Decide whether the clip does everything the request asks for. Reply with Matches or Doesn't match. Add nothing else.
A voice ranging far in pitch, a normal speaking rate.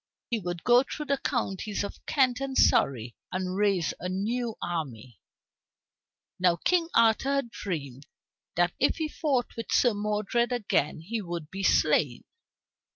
Matches